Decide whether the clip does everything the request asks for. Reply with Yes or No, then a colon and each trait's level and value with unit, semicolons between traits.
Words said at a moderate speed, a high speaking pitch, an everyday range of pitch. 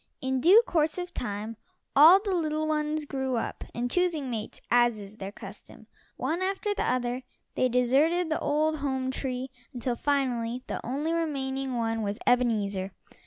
Yes: average, 165 wpm; very high, 265 Hz; average, 4.5 semitones